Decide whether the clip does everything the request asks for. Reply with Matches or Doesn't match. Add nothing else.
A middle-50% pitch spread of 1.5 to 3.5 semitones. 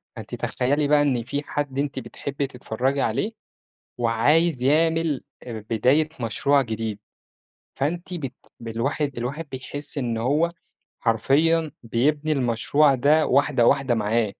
Doesn't match